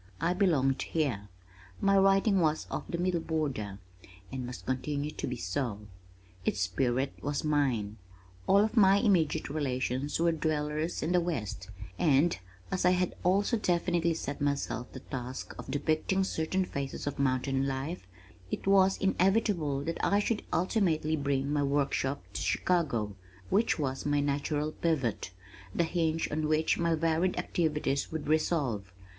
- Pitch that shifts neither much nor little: Yes, average, 4.3 semitones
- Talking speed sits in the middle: Yes, average, 150 wpm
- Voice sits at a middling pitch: Yes, medium, 155 Hz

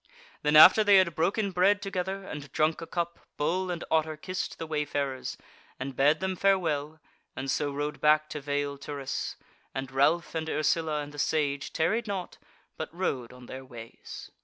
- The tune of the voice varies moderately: Yes, average, 4.0 semitones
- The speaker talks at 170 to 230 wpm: Yes, average, 175 wpm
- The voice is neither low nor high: Yes, medium, 155 Hz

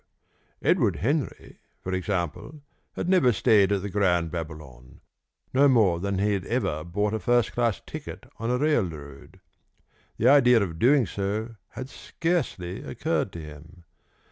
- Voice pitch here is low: Yes, low, 100 Hz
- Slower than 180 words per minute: Yes, average, 145 wpm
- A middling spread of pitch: No, wide, 6.1 semitones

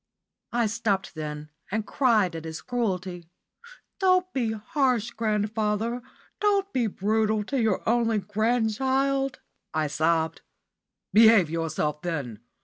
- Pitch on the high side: Yes, high, 215 Hz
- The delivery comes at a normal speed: No, slow, 115 wpm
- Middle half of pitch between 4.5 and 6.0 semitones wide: Yes, wide, 5.5 semitones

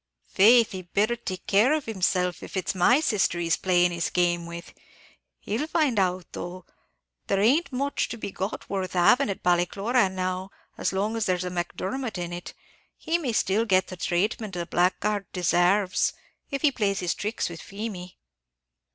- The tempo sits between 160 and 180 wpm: Yes, average, 175 wpm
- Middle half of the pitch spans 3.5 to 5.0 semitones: Yes, average, 3.9 semitones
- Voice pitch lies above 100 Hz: Yes, high, 190 Hz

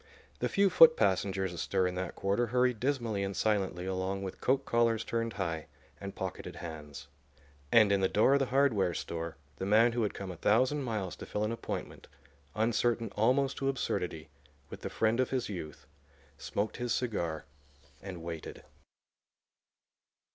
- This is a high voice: No, low, 105 Hz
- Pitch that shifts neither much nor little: Yes, average, 4.5 semitones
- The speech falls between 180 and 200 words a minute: No, average, 165 wpm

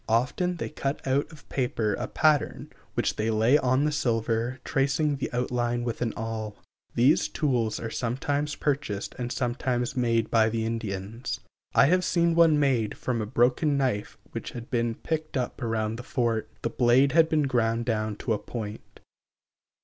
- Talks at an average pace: Yes, average, 170 wpm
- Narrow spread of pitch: No, average, 3.8 semitones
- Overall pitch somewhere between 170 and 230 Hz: No, low, 120 Hz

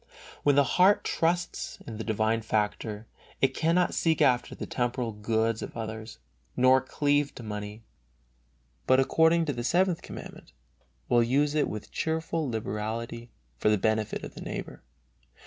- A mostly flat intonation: No, average, 5.1 semitones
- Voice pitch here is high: No, low, 120 Hz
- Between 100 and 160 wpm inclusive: Yes, average, 150 wpm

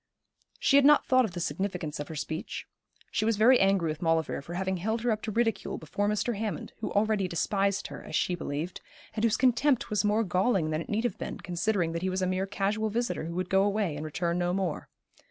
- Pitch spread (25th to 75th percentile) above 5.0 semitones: No, average, 4.1 semitones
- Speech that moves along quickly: Yes, fast, 235 wpm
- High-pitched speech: Yes, high, 195 Hz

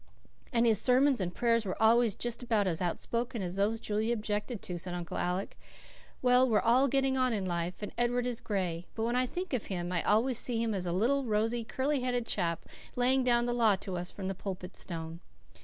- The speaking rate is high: Yes, fast, 215 wpm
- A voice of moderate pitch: No, high, 225 Hz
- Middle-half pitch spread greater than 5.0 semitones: No, average, 4.5 semitones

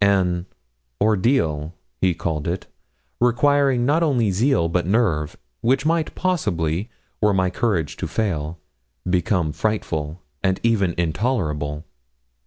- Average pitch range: No, wide, 6.4 semitones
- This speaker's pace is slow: Yes, slow, 115 wpm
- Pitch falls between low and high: No, very low, 95 Hz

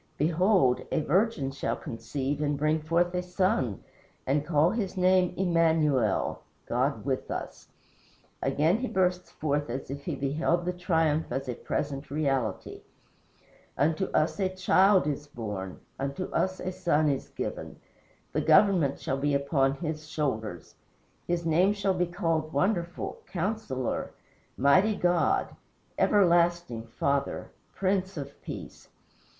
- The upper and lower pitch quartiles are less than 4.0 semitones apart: No, average, 4.5 semitones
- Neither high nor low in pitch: Yes, medium, 155 Hz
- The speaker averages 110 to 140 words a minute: Yes, slow, 135 wpm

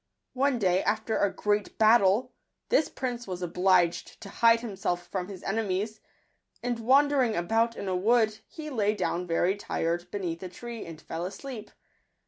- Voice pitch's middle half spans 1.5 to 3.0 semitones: No, average, 4.4 semitones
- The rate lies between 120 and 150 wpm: No, average, 160 wpm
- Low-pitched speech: No, high, 205 Hz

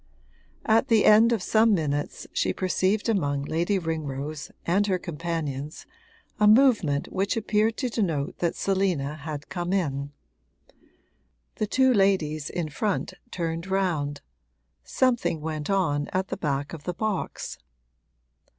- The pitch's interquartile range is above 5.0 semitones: Yes, wide, 5.5 semitones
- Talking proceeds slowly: Yes, slow, 130 wpm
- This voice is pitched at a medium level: Yes, medium, 175 Hz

